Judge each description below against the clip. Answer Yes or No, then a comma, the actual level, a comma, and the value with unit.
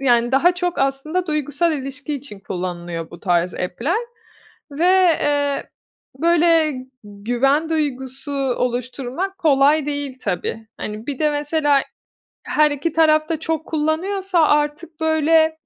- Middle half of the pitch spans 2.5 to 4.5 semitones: Yes, average, 3.8 semitones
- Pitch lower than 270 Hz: No, very high, 290 Hz